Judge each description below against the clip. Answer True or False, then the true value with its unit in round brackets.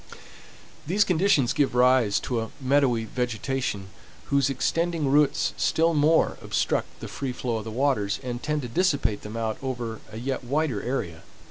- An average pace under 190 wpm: True (160 wpm)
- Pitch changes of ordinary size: True (4.2 semitones)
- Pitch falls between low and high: False (130 Hz)